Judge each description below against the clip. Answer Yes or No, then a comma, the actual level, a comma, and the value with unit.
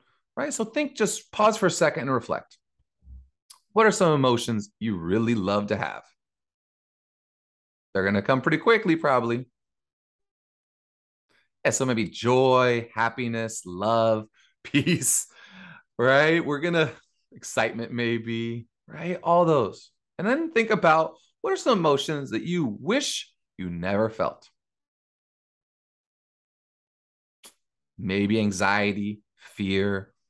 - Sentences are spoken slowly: Yes, slow, 115 wpm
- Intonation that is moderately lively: No, wide, 8.6 semitones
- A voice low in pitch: Yes, low, 115 Hz